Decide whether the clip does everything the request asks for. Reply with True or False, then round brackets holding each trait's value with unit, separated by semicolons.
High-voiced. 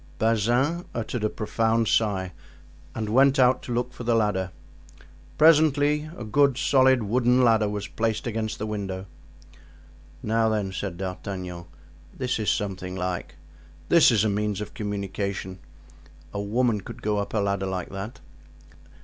False (110 Hz)